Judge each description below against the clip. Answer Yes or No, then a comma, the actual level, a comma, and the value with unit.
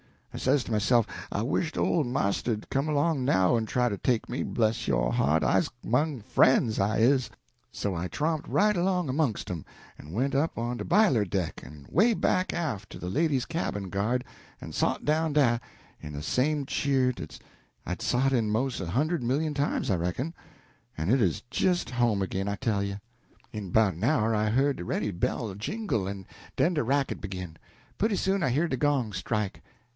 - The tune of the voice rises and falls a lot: Yes, wide, 6.5 semitones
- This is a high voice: No, low, 120 Hz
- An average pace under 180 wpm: No, average, 195 wpm